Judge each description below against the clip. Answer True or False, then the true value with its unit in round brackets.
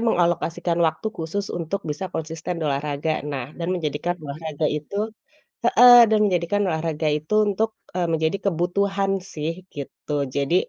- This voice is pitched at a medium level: True (165 Hz)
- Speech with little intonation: False (3.9 semitones)